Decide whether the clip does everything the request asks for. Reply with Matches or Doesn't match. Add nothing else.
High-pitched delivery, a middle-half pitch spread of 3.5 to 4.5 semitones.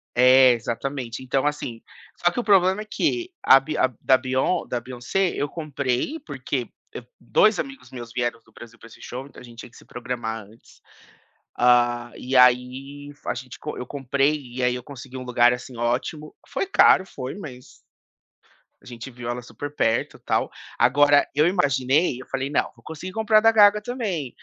Doesn't match